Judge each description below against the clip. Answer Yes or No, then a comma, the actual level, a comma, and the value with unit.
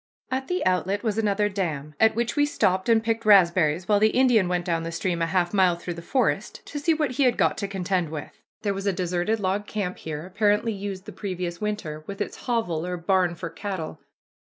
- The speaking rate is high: Yes, fast, 225 wpm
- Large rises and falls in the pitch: No, average, 3.6 semitones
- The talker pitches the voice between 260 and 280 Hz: No, high, 195 Hz